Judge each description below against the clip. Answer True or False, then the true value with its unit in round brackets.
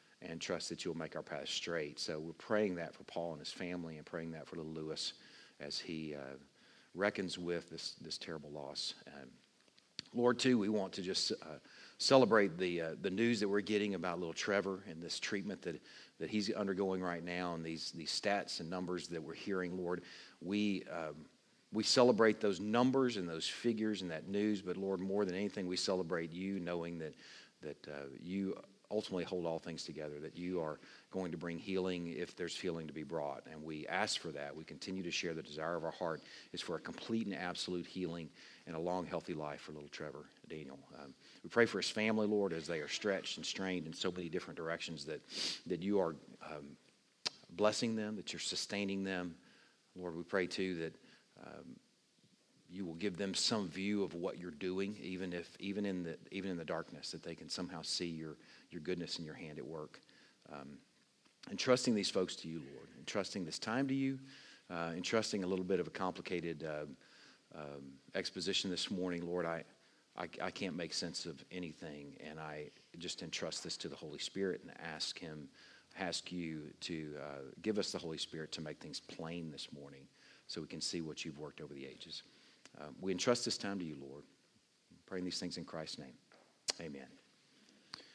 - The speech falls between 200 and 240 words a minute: True (205 wpm)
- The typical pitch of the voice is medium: False (90 Hz)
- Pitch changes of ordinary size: True (3.3 semitones)